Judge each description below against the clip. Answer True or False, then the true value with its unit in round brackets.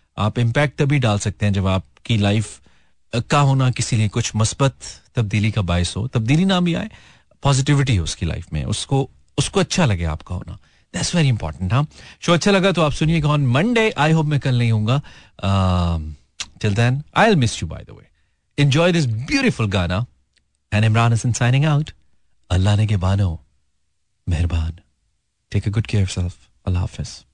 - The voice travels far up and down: True (7.6 semitones)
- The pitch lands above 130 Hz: False (110 Hz)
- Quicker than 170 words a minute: True (180 wpm)